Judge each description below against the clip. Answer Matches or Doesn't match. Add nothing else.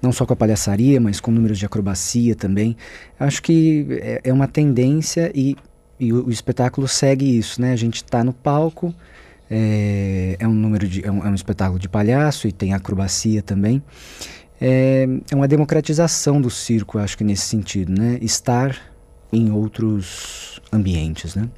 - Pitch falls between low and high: Doesn't match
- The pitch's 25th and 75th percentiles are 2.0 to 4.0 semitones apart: Doesn't match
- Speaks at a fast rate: Doesn't match